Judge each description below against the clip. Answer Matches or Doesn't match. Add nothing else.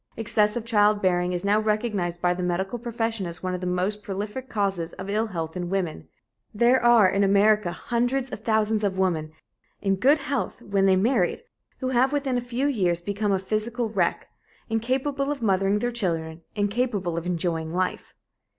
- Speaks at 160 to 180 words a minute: Matches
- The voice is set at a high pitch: Matches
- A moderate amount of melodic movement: Matches